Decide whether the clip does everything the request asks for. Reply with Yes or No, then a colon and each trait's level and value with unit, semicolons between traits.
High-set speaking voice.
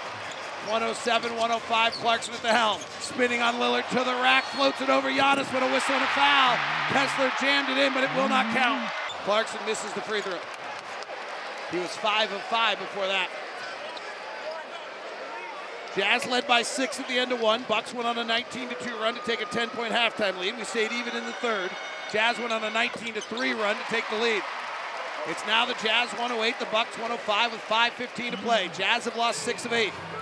Yes: high, 235 Hz